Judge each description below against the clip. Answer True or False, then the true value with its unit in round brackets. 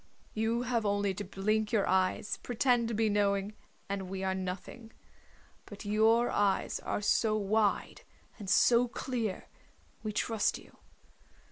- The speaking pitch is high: True (210 Hz)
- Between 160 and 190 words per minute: False (140 wpm)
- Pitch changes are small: True (2.3 semitones)